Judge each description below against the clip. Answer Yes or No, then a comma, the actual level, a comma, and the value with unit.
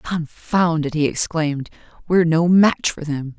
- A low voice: No, medium, 160 Hz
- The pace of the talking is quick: No, average, 160 wpm